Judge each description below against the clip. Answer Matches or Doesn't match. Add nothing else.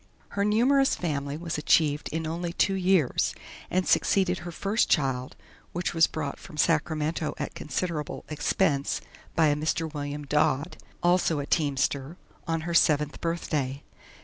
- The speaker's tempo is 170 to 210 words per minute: Doesn't match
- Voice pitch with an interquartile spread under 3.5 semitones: Matches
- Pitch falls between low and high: Matches